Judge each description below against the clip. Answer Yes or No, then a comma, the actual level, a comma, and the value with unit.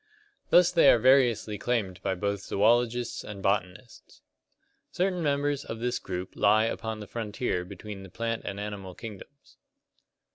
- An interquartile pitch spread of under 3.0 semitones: No, average, 3.6 semitones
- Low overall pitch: Yes, low, 110 Hz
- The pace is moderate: Yes, average, 145 wpm